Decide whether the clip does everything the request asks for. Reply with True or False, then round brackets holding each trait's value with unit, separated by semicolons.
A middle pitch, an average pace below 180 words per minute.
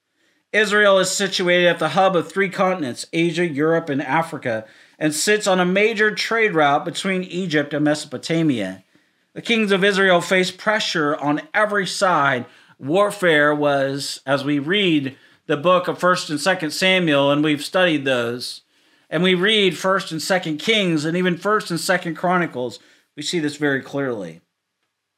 True (170 Hz; 160 wpm)